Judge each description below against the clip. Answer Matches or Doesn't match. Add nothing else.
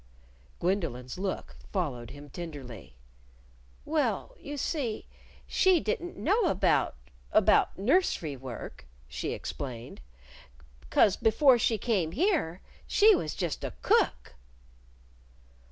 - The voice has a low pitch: Doesn't match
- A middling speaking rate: Doesn't match